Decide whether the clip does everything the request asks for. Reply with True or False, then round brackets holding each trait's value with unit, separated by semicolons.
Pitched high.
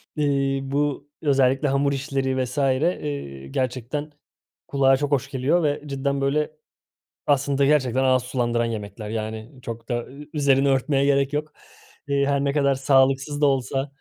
False (135 Hz)